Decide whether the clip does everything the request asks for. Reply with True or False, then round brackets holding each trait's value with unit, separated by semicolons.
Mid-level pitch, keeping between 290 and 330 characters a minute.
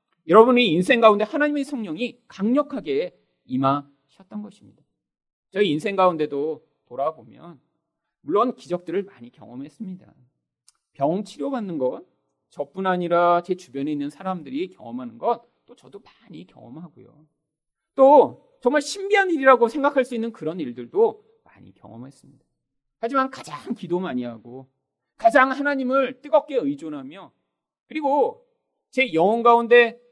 False (215 Hz; 305 characters per minute)